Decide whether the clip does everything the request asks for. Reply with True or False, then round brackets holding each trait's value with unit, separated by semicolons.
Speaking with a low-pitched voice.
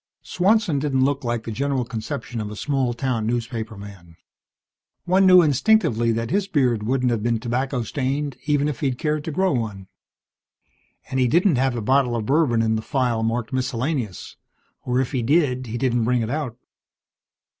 True (125 Hz)